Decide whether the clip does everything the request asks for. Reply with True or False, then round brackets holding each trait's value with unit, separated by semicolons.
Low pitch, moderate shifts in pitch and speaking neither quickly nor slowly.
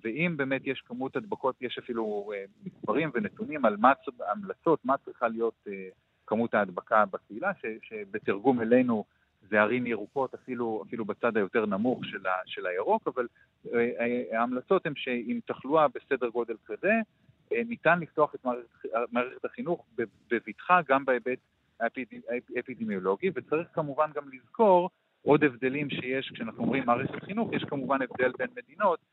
True (125 Hz; 4.7 semitones; 140 wpm)